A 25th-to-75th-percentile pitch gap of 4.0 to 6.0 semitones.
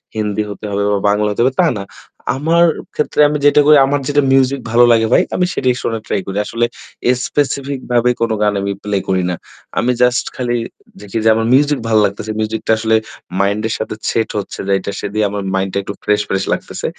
Yes: average, 4.3 semitones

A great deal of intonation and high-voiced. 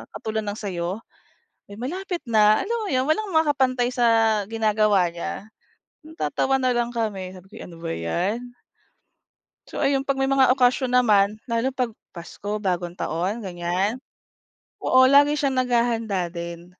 Yes: wide, 5.7 semitones; high, 225 Hz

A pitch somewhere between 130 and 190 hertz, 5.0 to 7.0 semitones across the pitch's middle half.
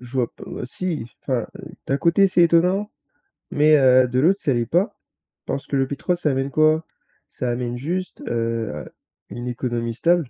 Yes: low, 135 Hz; wide, 5.6 semitones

